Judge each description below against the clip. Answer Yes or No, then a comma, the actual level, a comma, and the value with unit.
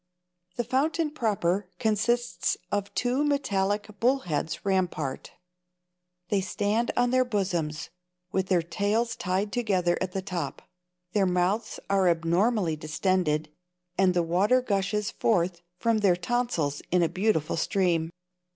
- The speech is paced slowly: Yes, slow, 125 wpm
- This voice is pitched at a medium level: No, high, 195 Hz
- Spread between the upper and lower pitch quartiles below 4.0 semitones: No, average, 4.5 semitones